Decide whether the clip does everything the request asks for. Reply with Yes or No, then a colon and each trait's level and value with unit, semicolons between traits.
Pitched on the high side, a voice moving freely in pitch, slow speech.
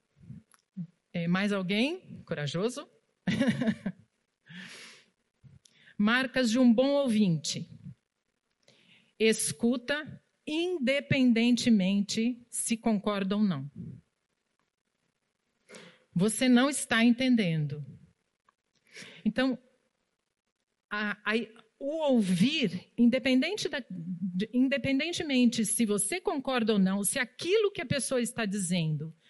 No: high, 225 Hz; average, 4.7 semitones; slow, 80 wpm